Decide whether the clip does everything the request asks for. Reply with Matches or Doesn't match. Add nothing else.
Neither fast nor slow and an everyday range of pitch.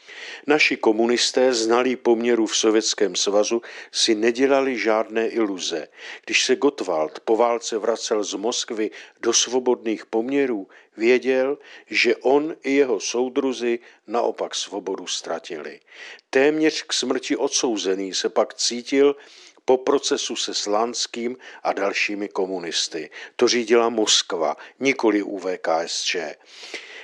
Doesn't match